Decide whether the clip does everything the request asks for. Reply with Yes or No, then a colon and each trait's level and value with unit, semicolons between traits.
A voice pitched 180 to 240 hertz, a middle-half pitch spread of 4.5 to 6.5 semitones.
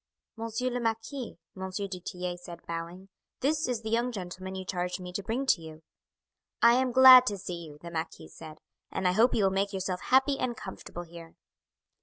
Yes: high, 190 Hz; average, 5.1 semitones